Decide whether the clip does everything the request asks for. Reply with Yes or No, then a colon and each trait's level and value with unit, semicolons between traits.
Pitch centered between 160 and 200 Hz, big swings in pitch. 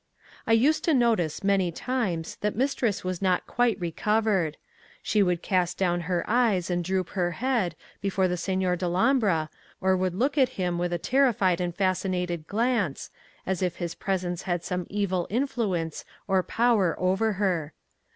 No: medium, 185 Hz; average, 3.9 semitones